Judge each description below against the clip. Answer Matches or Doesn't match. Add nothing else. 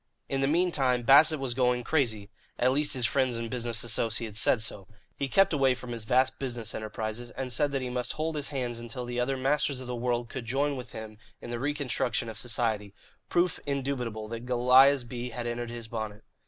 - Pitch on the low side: Matches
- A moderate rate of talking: Doesn't match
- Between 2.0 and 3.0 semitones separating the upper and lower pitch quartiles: Matches